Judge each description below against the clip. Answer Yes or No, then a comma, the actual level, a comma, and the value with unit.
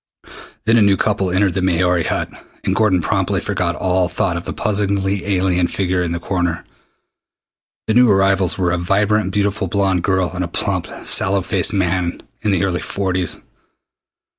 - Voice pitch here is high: No, very low, 95 Hz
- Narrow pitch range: Yes, narrow, 2.0 semitones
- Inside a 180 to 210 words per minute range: No, average, 170 wpm